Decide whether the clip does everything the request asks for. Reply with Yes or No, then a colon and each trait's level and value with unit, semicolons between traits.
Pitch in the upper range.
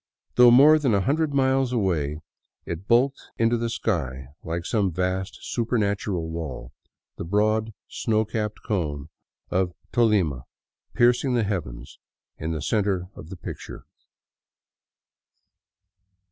No: low, 100 Hz